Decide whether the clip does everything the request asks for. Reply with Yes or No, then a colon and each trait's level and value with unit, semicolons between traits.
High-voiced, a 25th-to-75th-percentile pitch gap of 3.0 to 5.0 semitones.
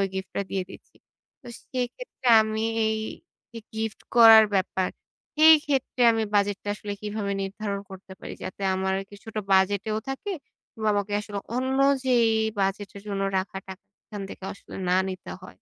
No: high, 205 Hz; narrow, 2.5 semitones